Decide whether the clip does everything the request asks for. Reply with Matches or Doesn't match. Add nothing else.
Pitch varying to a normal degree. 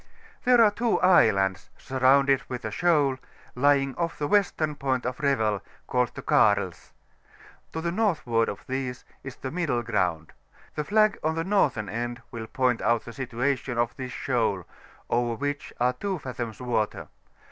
Matches